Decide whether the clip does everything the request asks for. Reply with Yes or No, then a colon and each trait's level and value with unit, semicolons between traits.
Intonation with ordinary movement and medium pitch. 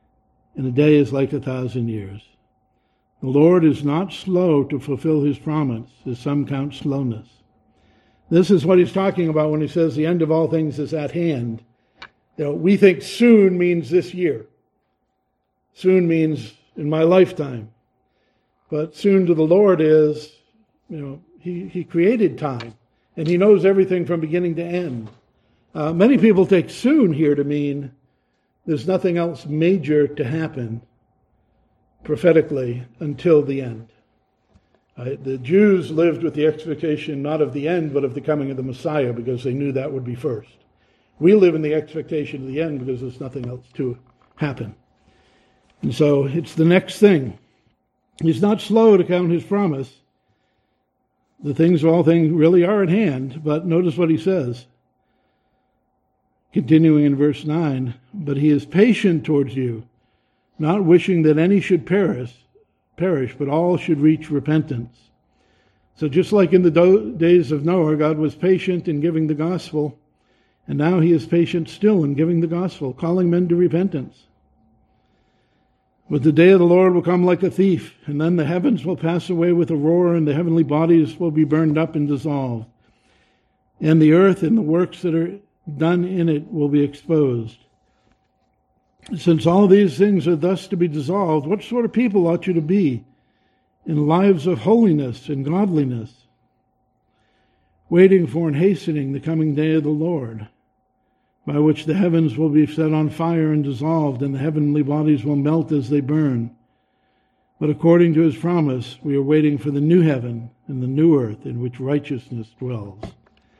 Yes: average, 4.5 semitones; medium, 155 Hz